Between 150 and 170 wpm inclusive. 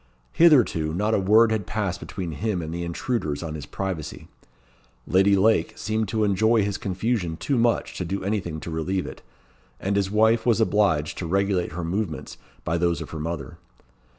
No: average, 180 wpm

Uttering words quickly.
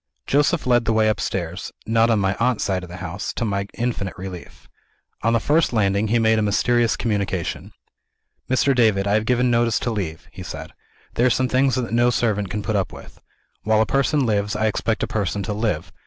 Yes: fast, 215 wpm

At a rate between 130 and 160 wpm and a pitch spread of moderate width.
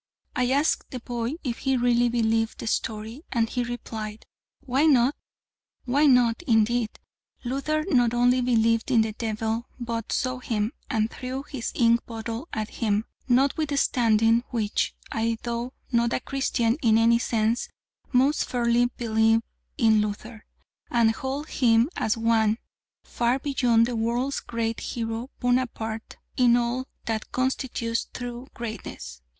No: average, 140 wpm; narrow, 2.0 semitones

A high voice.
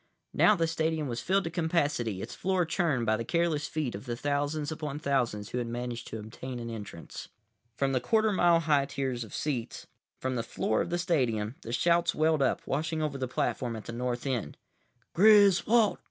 No: medium, 140 Hz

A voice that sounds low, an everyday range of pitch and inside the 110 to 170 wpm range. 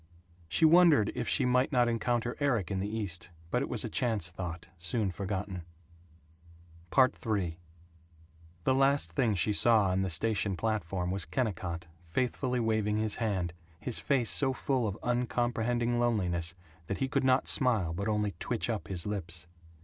Yes: low, 110 Hz; average, 4.7 semitones; average, 160 wpm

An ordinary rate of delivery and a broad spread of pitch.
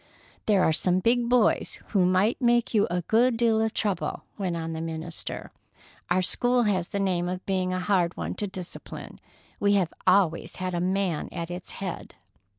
No: average, 185 wpm; average, 3.2 semitones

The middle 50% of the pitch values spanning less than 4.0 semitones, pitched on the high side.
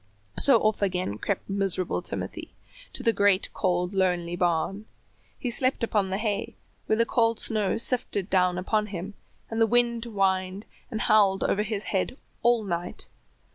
Yes: average, 3.3 semitones; high, 200 Hz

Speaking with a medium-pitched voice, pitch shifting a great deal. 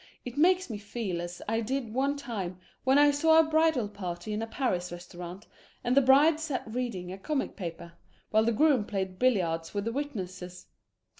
No: high, 225 Hz; wide, 7.1 semitones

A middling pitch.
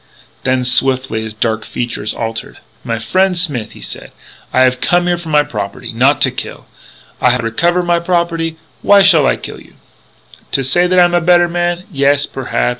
Yes: medium, 150 Hz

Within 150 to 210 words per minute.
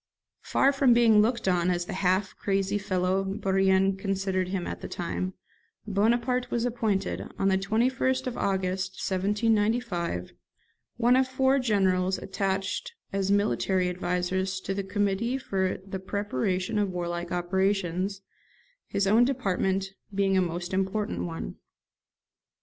No: slow, 135 wpm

